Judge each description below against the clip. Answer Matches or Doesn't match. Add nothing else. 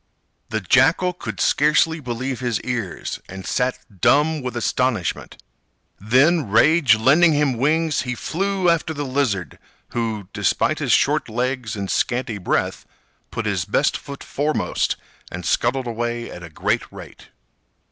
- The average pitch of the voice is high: Doesn't match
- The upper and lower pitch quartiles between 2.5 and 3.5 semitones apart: Doesn't match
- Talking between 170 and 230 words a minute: Doesn't match